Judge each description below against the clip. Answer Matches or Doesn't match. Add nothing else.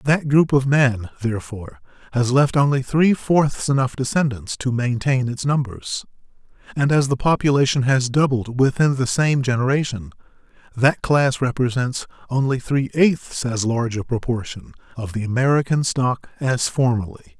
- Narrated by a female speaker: Doesn't match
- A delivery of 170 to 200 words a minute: Doesn't match